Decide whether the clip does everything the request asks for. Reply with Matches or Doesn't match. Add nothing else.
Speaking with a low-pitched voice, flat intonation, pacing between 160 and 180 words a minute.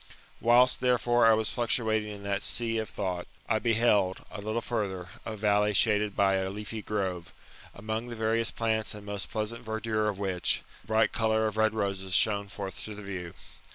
Doesn't match